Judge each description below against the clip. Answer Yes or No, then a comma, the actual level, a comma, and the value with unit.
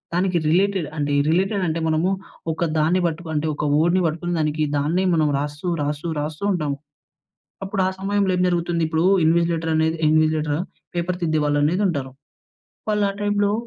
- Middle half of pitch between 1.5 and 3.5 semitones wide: Yes, average, 3.0 semitones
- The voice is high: No, medium, 165 Hz